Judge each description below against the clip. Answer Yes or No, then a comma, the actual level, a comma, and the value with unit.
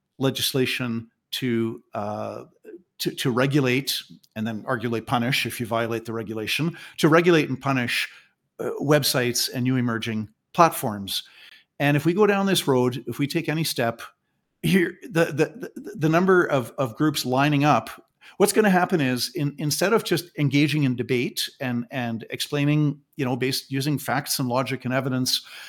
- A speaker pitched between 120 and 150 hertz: Yes, low, 135 Hz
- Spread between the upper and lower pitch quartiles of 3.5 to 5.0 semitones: Yes, average, 3.8 semitones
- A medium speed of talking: Yes, average, 170 wpm